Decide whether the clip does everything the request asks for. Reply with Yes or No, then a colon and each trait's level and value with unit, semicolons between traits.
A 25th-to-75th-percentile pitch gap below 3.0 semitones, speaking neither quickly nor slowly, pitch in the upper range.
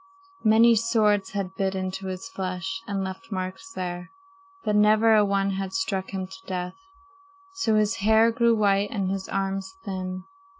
Yes: narrow, 2.5 semitones; average, 165 wpm; high, 195 Hz